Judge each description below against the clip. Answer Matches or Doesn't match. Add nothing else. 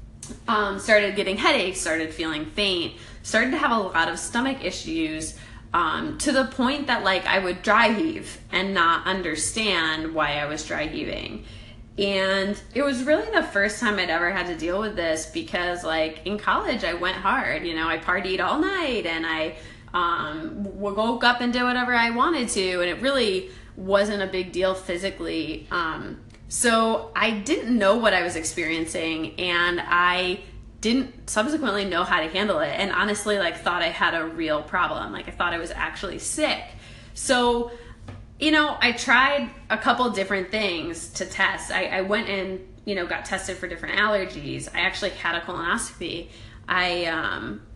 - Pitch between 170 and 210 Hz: Matches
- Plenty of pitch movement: Matches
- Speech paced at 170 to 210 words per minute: Matches